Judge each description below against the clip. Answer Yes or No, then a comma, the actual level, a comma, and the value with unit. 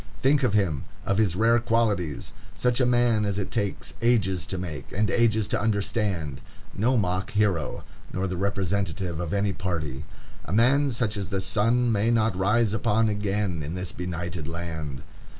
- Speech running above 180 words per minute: No, average, 165 wpm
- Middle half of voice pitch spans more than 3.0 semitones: Yes, average, 4.0 semitones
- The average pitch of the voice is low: Yes, low, 100 Hz